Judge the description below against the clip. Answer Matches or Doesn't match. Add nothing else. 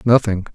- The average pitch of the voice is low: Matches